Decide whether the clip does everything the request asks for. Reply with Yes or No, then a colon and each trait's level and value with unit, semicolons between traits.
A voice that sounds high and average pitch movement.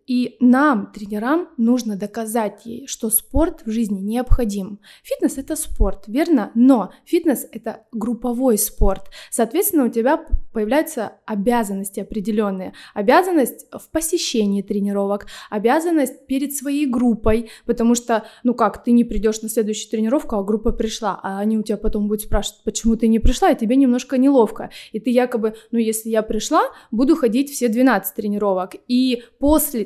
Yes: high, 230 Hz; average, 3.5 semitones